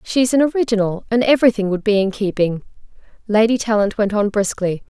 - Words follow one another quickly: No, average, 170 wpm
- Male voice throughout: No, female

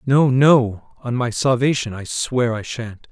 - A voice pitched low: Yes, low, 125 Hz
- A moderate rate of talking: Yes, average, 175 wpm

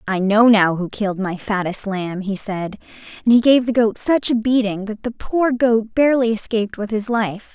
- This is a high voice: Yes, high, 215 Hz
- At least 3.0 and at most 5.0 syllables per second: Yes, 4.9 syllables/s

